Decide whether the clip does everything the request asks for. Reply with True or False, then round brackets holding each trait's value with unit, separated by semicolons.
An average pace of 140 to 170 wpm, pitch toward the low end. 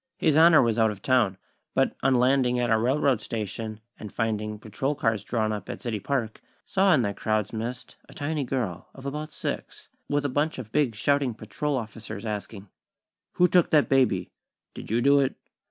False (190 wpm; 120 Hz)